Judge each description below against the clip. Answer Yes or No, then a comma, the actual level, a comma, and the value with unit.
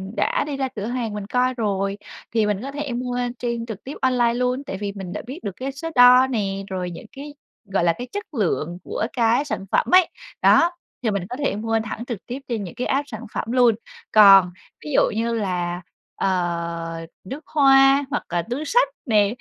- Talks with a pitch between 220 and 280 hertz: Yes, high, 230 Hz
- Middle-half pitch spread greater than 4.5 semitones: Yes, average, 4.9 semitones